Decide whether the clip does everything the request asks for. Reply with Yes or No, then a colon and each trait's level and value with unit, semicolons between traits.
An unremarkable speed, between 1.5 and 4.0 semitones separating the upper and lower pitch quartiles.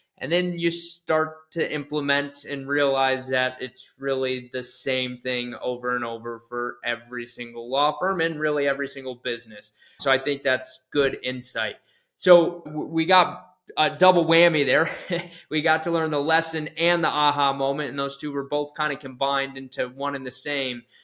Yes: average, 185 wpm; average, 3.6 semitones